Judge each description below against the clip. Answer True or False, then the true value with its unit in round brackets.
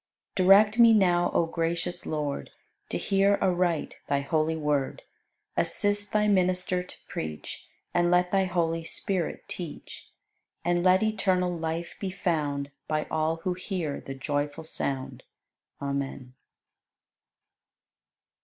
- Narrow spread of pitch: False (3.5 semitones)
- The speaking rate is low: True (125 wpm)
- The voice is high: False (175 Hz)